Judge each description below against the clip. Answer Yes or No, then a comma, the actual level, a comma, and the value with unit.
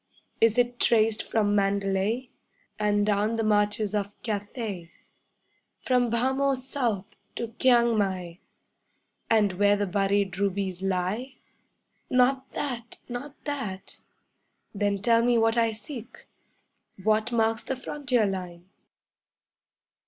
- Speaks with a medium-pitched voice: No, high, 215 Hz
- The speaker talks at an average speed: No, slow, 115 wpm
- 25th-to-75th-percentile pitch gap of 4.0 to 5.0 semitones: No, average, 3.2 semitones